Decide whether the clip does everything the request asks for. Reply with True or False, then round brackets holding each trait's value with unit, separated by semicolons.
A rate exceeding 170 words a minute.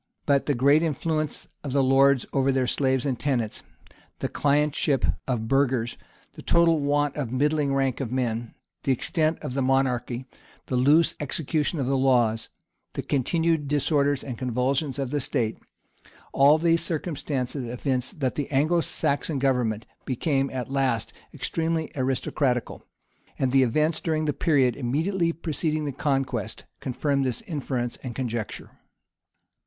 False (150 wpm)